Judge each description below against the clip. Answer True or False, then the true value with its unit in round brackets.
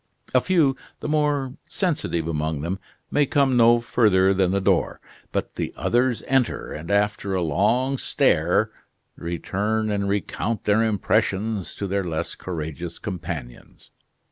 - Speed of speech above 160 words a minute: False (140 wpm)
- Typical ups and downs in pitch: False (5.8 semitones)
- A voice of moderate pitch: False (100 Hz)